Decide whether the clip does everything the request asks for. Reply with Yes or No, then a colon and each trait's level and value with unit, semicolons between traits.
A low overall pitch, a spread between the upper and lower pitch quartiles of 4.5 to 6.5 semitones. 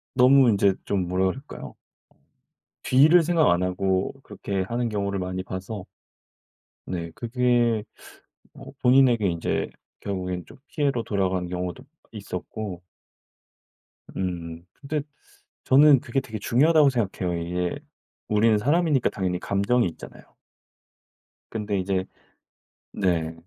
Yes: low, 100 Hz; average, 5.3 semitones